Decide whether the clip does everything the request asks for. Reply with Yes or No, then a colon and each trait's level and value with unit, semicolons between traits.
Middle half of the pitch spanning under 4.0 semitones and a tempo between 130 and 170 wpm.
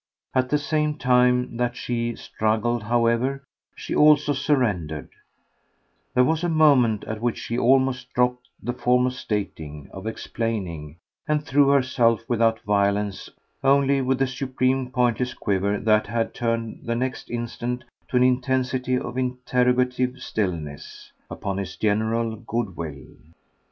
Yes: average, 2.8 semitones; slow, 135 wpm